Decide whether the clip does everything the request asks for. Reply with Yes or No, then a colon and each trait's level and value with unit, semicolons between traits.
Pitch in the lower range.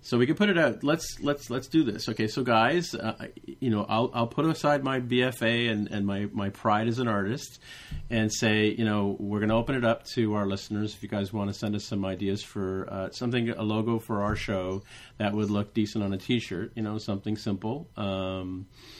Yes: low, 110 Hz